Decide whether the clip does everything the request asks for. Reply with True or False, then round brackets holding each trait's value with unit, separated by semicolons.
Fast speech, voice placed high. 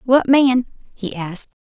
False (145 wpm; 240 Hz)